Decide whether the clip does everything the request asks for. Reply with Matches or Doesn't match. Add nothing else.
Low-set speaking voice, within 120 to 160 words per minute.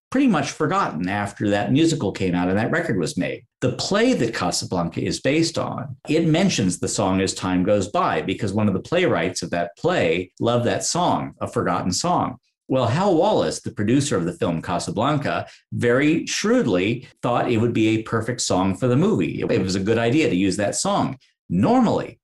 Doesn't match